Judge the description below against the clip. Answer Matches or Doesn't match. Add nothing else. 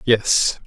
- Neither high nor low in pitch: Doesn't match